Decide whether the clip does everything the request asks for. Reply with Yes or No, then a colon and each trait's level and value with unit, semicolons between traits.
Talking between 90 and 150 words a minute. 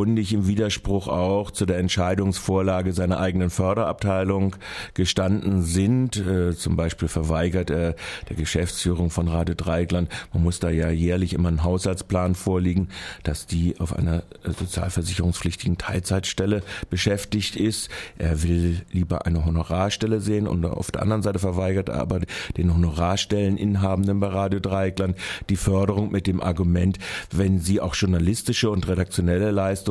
Yes: average, 135 wpm